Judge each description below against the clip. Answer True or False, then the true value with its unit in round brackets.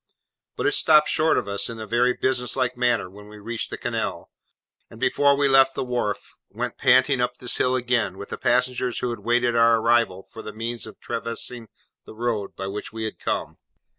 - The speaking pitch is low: True (120 Hz)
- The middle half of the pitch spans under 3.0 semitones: True (2.4 semitones)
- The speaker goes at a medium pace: False (210 wpm)